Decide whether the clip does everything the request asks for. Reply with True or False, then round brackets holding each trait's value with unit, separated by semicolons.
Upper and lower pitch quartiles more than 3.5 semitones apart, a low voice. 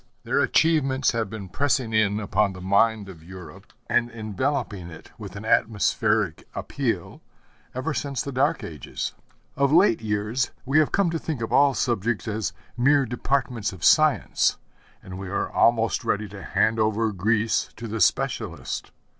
True (4.5 semitones; 110 Hz)